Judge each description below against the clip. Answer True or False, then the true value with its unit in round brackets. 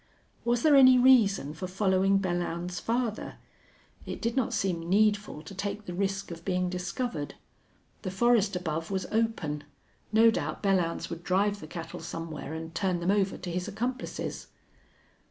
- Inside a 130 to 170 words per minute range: True (155 wpm)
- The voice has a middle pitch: False (195 Hz)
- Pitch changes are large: False (3.8 semitones)